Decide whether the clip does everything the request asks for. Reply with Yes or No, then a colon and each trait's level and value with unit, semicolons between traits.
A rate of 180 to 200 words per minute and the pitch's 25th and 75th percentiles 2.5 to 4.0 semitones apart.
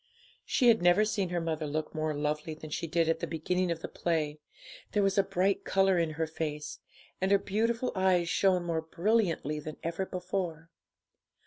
Yes: average, 190 wpm; average, 3.5 semitones